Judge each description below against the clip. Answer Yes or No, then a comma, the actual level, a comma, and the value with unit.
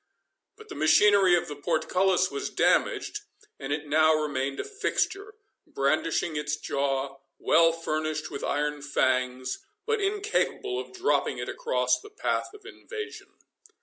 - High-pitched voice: No, medium, 155 Hz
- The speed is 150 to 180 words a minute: No, average, 140 wpm